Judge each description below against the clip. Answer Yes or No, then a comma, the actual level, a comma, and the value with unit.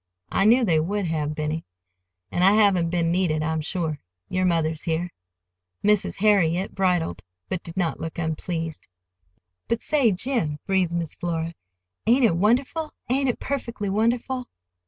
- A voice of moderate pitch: Yes, medium, 180 Hz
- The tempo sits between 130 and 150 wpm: Yes, average, 140 wpm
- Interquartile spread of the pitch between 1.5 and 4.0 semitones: No, average, 4.7 semitones